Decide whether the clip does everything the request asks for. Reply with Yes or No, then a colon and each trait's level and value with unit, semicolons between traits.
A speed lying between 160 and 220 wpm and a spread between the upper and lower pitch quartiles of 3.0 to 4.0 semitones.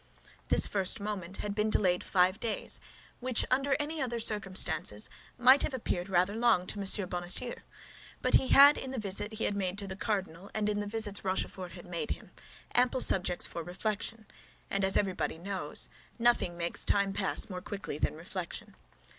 Yes: average, 180 wpm; average, 3.5 semitones